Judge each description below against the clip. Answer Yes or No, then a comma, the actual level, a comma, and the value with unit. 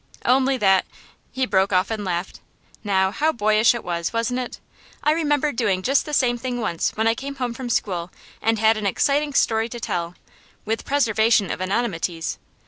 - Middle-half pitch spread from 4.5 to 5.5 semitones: Yes, average, 5.0 semitones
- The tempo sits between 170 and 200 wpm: Yes, average, 190 wpm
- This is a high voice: Yes, high, 225 Hz